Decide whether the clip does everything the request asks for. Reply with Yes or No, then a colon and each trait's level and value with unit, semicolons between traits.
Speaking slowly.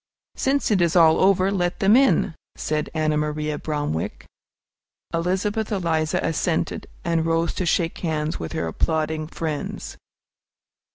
Yes: slow, 130 wpm